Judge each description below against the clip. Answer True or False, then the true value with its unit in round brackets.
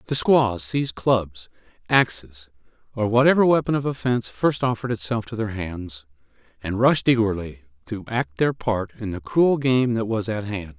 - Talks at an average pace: True (170 wpm)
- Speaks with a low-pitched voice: True (110 Hz)